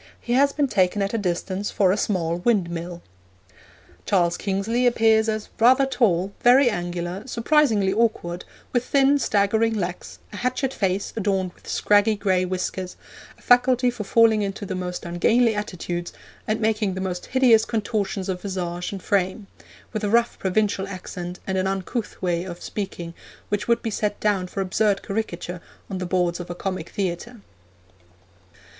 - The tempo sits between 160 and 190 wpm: Yes, average, 165 wpm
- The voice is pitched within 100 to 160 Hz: No, high, 200 Hz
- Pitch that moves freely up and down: No, average, 3.7 semitones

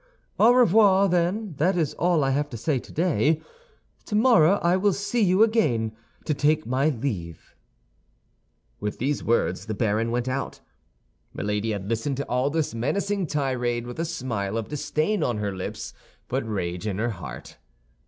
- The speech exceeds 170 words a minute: No, average, 165 wpm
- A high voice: No, medium, 140 Hz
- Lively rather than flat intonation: Yes, wide, 7.7 semitones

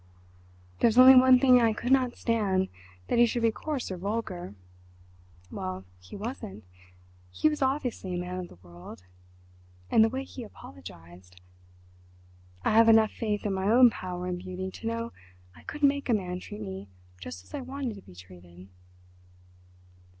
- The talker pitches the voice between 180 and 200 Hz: Yes, high, 190 Hz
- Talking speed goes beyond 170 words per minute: No, average, 165 wpm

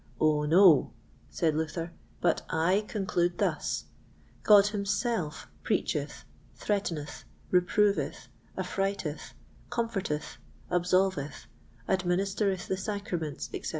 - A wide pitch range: No, average, 3.9 semitones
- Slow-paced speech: Yes, slow, 85 wpm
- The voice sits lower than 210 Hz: Yes, medium, 185 Hz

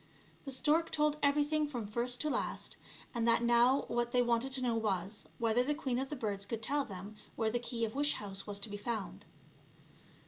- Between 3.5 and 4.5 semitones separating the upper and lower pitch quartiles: Yes, average, 4.1 semitones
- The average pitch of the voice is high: Yes, high, 240 Hz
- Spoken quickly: Yes, fast, 210 wpm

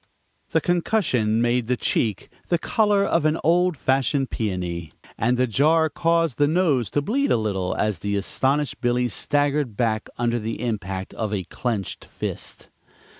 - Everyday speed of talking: Yes, average, 160 wpm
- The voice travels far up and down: Yes, wide, 6.2 semitones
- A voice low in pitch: Yes, low, 125 Hz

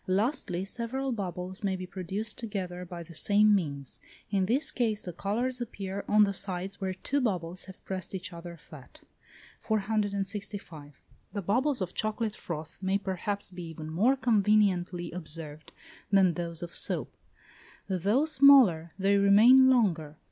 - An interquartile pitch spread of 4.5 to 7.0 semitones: No, average, 3.3 semitones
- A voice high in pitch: Yes, high, 195 Hz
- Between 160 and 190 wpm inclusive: No, average, 150 wpm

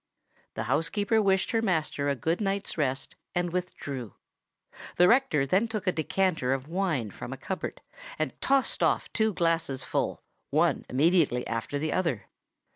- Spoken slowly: No, average, 155 wpm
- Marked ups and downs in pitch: Yes, wide, 6.0 semitones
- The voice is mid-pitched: Yes, medium, 165 Hz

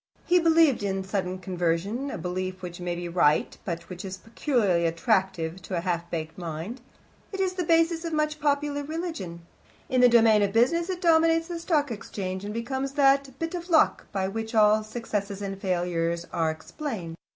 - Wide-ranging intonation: Yes, wide, 8.6 semitones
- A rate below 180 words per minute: No, average, 185 wpm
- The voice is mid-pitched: No, high, 210 Hz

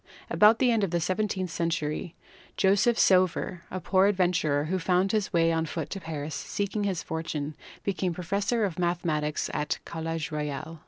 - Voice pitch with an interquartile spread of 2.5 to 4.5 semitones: Yes, average, 3.4 semitones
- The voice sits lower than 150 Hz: No, medium, 175 Hz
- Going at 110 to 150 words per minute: No, average, 170 wpm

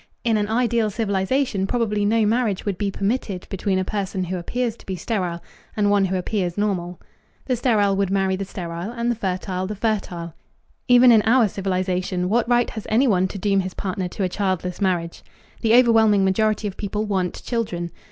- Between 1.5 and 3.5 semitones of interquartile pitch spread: Yes, average, 3.1 semitones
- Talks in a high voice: Yes, high, 200 Hz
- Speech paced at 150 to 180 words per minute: No, average, 190 wpm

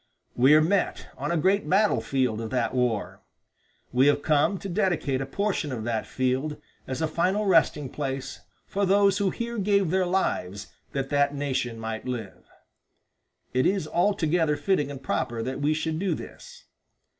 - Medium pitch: Yes, medium, 150 Hz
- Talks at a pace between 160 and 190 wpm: Yes, average, 170 wpm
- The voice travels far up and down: Yes, wide, 6.5 semitones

